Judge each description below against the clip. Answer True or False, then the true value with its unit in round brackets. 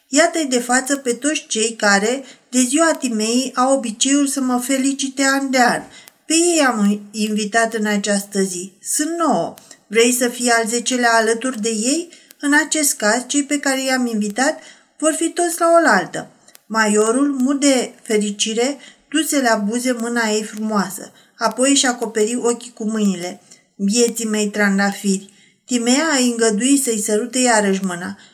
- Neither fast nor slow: True (155 wpm)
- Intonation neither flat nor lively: True (4.2 semitones)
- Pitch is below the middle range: False (240 Hz)